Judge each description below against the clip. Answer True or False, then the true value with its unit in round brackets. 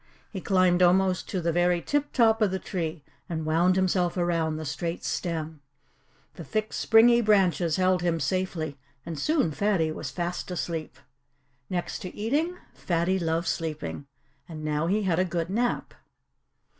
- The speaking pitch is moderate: True (175 Hz)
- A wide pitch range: False (2.7 semitones)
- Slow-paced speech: False (155 wpm)